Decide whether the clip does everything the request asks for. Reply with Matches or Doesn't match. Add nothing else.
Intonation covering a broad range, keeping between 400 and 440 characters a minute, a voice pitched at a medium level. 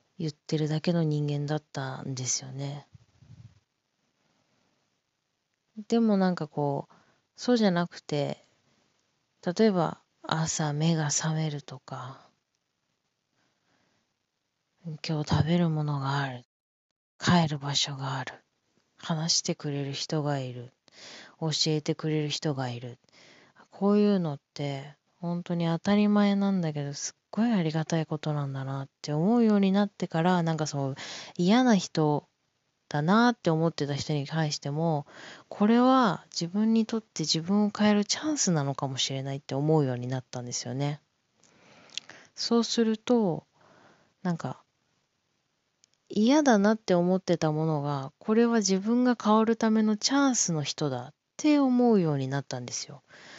Doesn't match